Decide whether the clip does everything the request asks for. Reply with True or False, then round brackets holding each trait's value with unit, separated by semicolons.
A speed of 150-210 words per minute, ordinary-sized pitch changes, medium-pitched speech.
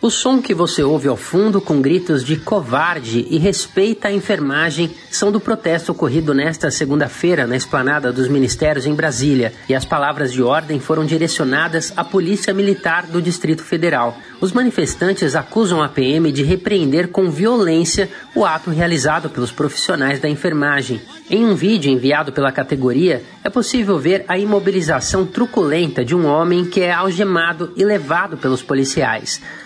True (160 wpm; 5.0 semitones; 165 Hz)